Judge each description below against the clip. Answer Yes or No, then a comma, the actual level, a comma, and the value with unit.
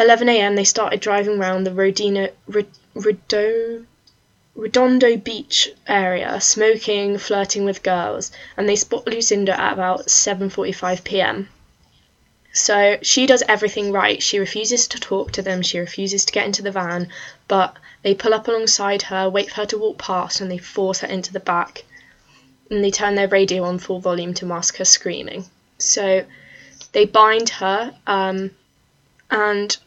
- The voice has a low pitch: No, high, 200 Hz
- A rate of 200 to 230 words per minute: No, average, 155 wpm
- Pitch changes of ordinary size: No, narrow, 2.1 semitones